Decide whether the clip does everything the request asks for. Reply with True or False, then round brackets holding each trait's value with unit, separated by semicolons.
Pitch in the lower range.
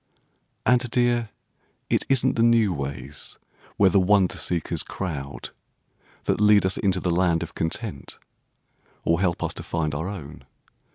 True (95 Hz)